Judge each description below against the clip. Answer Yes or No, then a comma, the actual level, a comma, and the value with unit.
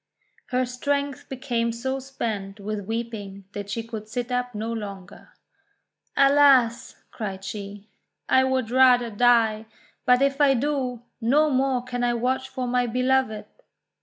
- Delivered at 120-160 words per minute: Yes, average, 140 wpm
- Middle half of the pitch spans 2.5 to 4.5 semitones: Yes, average, 3.1 semitones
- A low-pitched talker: No, high, 245 Hz